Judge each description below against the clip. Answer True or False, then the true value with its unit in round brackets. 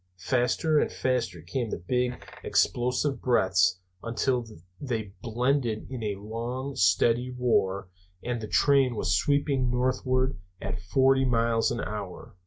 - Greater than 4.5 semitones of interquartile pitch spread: False (3.5 semitones)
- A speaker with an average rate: False (130 wpm)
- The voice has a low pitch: True (120 Hz)